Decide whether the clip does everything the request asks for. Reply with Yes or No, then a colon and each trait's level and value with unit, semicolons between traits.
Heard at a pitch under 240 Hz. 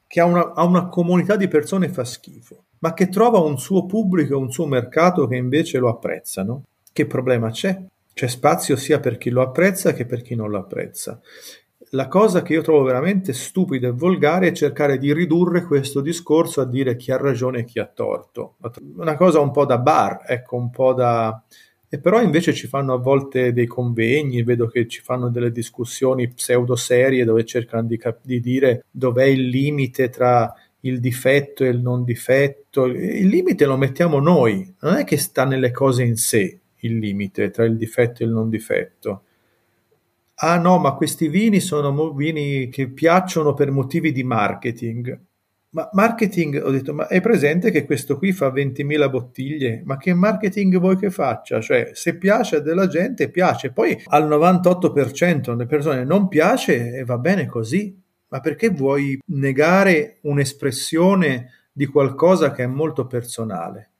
Yes: medium, 140 Hz